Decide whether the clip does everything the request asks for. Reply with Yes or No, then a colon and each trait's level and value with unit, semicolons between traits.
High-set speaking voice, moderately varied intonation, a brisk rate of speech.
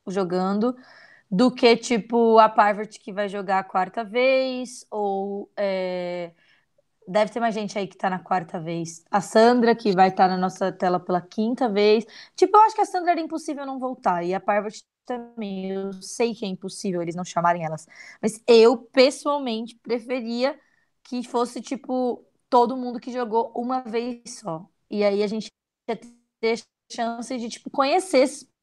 No: high, 230 Hz; average, 4.3 semitones; average, 175 wpm